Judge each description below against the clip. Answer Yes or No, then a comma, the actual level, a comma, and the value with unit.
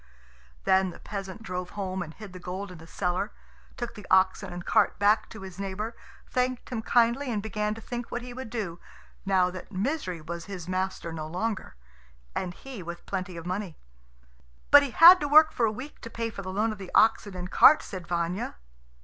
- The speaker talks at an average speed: No, fast, 210 wpm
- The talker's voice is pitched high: Yes, high, 195 Hz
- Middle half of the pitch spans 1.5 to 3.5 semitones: No, average, 4.0 semitones